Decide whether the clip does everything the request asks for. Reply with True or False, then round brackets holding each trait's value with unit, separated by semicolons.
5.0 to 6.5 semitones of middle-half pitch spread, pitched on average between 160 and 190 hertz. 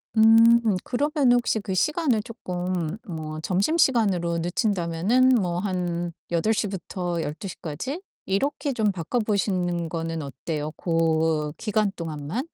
True (5.3 semitones; 185 Hz)